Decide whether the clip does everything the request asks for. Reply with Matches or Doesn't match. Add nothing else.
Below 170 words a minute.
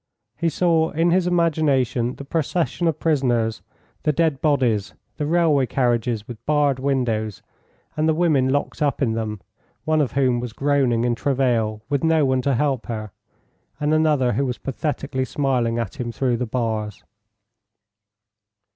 Matches